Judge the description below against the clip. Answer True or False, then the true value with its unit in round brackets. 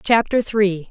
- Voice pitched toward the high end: True (205 Hz)